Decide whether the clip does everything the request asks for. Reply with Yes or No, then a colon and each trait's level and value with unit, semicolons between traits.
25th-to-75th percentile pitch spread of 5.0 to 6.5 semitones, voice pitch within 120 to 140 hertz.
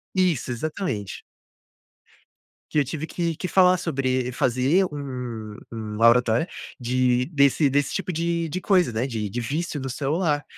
Yes: average, 5.3 semitones; low, 135 Hz